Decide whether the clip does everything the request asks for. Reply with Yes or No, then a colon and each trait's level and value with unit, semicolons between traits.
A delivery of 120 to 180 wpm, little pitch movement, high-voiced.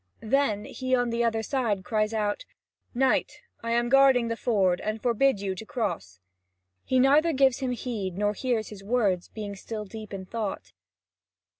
No: average, 170 wpm; average, 3.4 semitones; high, 225 Hz